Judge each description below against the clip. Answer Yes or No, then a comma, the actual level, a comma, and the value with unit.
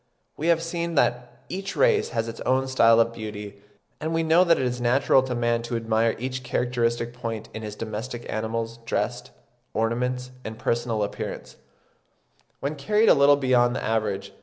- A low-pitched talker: Yes, low, 120 Hz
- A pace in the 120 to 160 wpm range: No, average, 175 wpm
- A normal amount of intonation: Yes, average, 3.0 semitones